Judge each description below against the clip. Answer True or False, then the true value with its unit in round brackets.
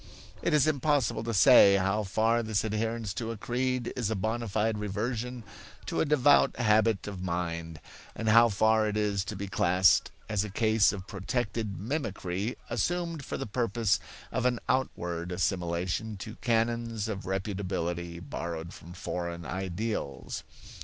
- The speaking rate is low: False (155 wpm)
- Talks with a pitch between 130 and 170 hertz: False (105 Hz)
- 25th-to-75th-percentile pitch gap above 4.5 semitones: False (3.8 semitones)